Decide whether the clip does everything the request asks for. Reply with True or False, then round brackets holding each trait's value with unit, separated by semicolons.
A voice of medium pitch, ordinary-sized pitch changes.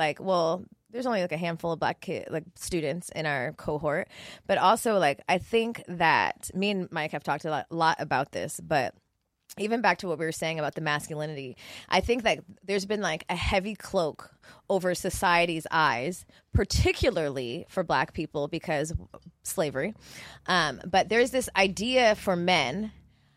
True (180 Hz; 4.3 semitones)